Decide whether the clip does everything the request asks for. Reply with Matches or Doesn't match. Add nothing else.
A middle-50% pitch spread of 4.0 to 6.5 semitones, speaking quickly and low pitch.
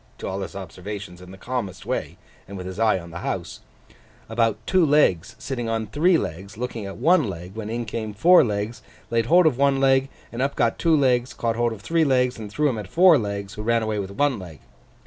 Matches